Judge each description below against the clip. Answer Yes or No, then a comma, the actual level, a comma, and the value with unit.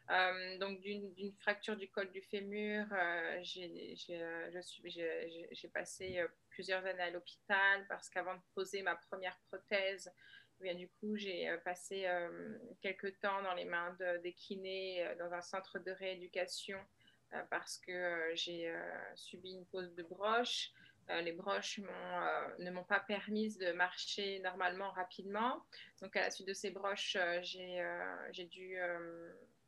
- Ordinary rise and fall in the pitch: No, narrow, 1.9 semitones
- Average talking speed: Yes, average, 170 wpm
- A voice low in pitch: No, medium, 185 Hz